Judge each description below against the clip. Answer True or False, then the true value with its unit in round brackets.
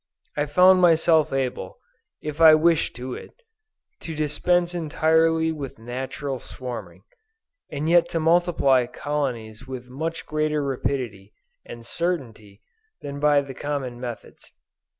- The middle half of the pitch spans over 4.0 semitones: True (4.4 semitones)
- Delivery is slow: True (120 wpm)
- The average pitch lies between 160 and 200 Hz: False (145 Hz)